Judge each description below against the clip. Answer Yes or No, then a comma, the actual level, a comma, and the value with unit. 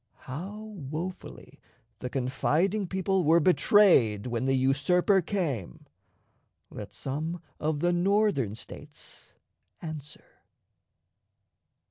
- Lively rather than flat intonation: Yes, wide, 6.0 semitones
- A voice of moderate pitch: Yes, medium, 160 Hz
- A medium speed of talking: No, slow, 90 wpm